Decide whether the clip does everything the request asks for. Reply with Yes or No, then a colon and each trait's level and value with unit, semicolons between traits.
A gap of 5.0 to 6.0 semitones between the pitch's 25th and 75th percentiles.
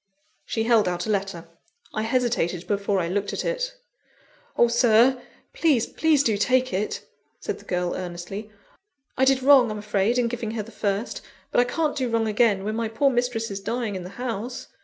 No: average, 3.7 semitones